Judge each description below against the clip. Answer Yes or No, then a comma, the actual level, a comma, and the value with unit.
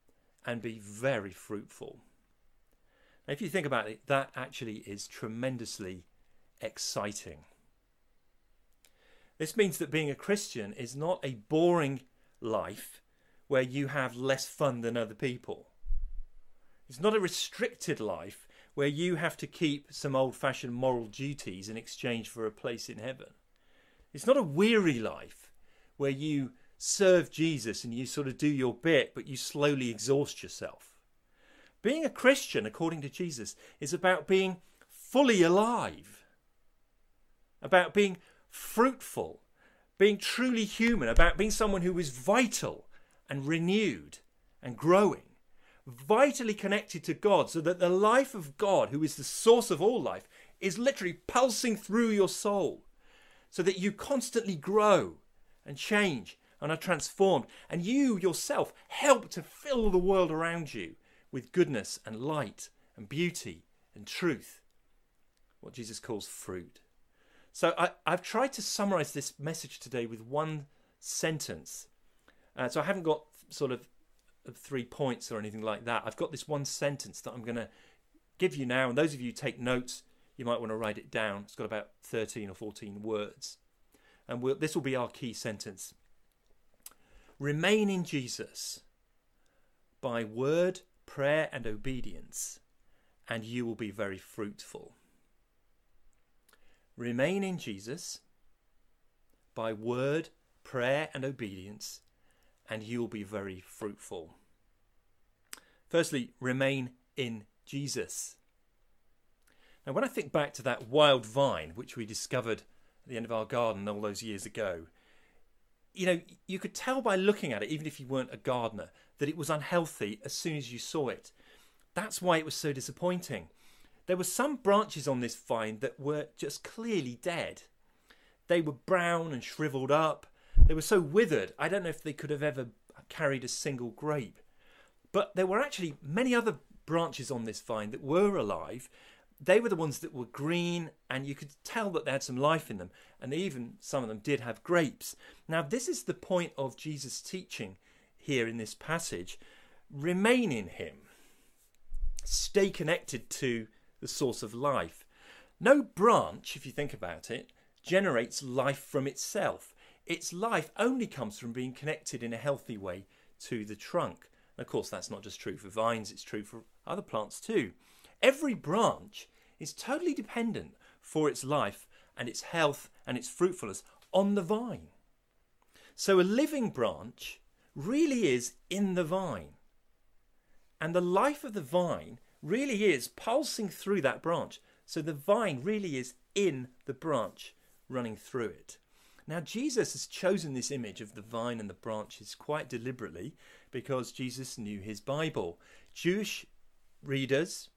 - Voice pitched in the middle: Yes, medium, 145 Hz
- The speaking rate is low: No, average, 155 wpm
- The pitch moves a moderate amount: No, wide, 7.1 semitones